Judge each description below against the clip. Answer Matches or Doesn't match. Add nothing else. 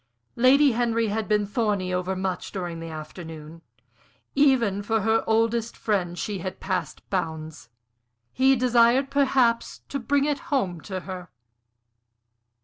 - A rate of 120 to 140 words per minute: Matches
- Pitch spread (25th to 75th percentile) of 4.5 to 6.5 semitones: Matches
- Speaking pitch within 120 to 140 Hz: Doesn't match